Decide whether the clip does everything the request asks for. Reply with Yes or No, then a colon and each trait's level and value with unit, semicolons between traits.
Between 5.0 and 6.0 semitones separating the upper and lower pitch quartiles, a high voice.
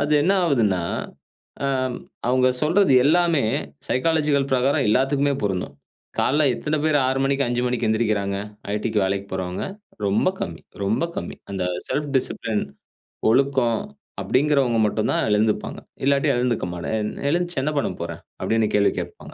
No: average, 5.3 semitones; low, 125 Hz